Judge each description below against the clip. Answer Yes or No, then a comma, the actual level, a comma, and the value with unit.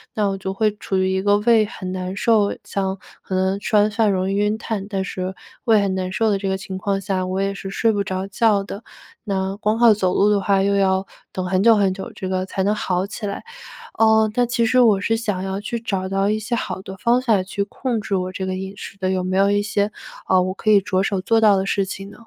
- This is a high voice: Yes, high, 195 Hz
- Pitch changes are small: Yes, narrow, 2.0 semitones